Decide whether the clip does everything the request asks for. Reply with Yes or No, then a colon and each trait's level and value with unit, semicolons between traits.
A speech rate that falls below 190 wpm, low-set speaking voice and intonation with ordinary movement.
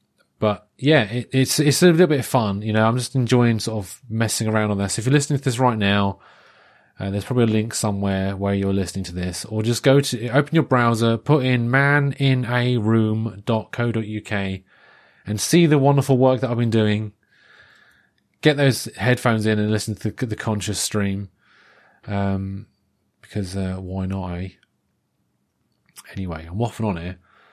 Yes: average, 175 wpm; low, 110 Hz; average, 4.3 semitones